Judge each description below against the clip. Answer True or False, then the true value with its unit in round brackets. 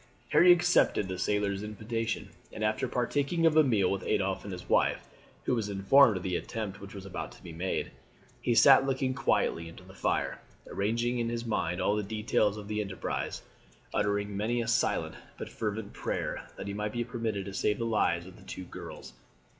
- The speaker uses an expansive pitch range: False (3.3 semitones)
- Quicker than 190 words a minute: True (200 wpm)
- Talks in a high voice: False (105 Hz)